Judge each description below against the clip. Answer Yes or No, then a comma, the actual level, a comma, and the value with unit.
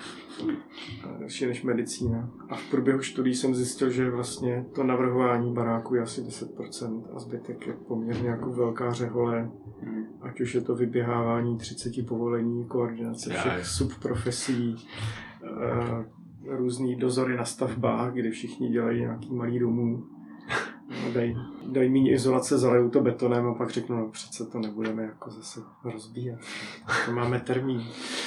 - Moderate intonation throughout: No, narrow, 1.4 semitones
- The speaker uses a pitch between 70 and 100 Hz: No, low, 120 Hz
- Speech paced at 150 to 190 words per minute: No, average, 140 wpm